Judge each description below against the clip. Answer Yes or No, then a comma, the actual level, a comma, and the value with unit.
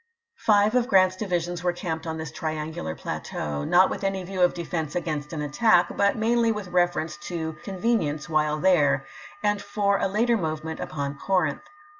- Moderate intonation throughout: Yes, average, 4.2 semitones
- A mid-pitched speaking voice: Yes, medium, 175 Hz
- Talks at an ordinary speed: Yes, average, 170 wpm